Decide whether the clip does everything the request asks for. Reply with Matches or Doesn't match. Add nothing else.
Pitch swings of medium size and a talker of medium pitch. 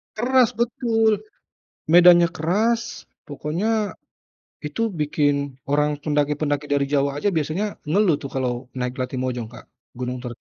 Doesn't match